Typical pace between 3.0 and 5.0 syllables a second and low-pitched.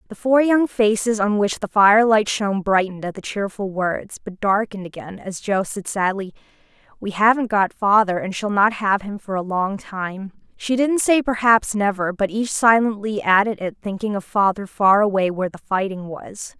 No: 4.9 syllables/s; high, 205 Hz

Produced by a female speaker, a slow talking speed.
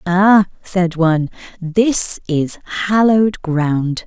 Yes: female; slow, 105 wpm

